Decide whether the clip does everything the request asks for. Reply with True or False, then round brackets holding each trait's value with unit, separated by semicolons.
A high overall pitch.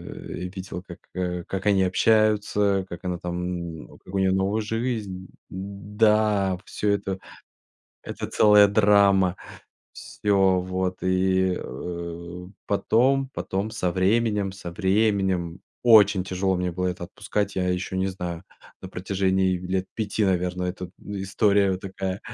False (95 Hz)